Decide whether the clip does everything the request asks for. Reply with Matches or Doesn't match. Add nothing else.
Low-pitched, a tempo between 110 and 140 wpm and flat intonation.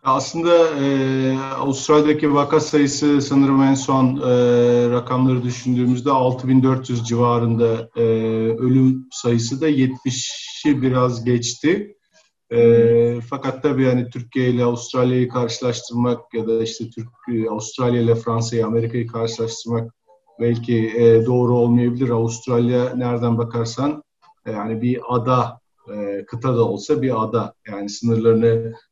Matches